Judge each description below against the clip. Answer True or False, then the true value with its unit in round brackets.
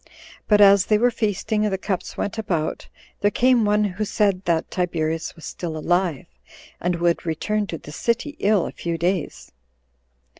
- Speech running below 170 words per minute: False (175 wpm)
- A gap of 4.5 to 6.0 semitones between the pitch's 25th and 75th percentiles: False (3.7 semitones)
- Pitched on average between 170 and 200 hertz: True (190 Hz)